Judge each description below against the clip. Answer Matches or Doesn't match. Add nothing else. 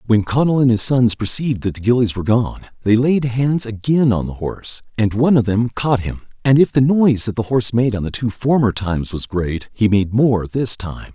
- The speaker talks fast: Matches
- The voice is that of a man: Matches